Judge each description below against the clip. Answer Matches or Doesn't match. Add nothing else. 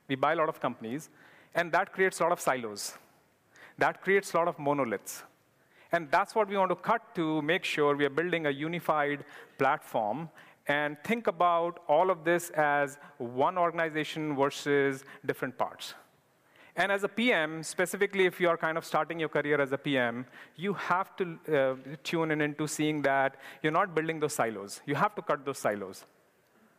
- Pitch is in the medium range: Matches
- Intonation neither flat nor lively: Matches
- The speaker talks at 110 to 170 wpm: Doesn't match